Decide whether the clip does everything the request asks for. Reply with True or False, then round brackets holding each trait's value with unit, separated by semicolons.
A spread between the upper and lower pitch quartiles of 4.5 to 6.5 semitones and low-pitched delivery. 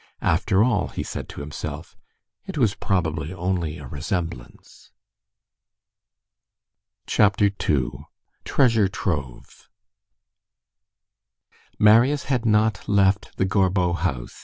True (4.8 semitones; 95 Hz)